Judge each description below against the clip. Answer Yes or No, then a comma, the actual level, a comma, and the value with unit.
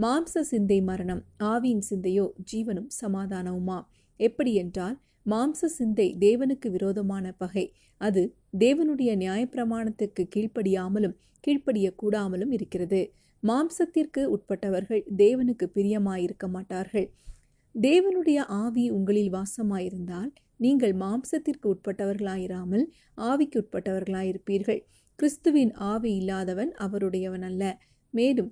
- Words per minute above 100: No, average, 85 wpm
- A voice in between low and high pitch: No, high, 205 Hz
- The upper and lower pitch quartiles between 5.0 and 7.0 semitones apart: No, average, 4.2 semitones